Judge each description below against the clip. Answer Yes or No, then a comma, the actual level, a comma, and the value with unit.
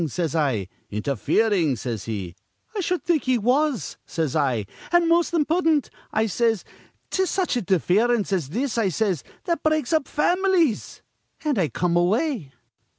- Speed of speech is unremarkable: Yes, average, 150 wpm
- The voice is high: Yes, high, 220 Hz